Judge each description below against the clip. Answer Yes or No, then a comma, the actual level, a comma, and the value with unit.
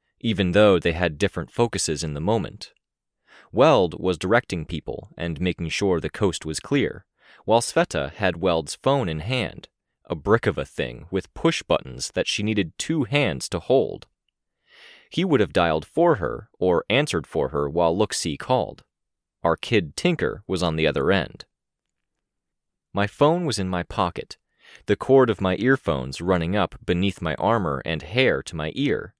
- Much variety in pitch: No, average, 4.3 semitones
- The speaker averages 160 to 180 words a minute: Yes, average, 175 wpm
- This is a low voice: Yes, very low, 90 Hz